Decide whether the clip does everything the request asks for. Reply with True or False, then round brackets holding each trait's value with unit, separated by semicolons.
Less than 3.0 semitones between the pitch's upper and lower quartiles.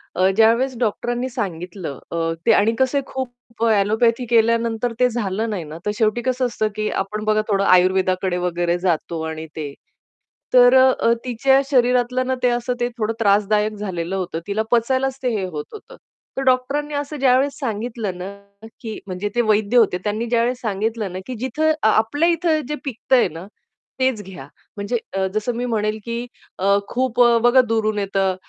False (4.0 semitones)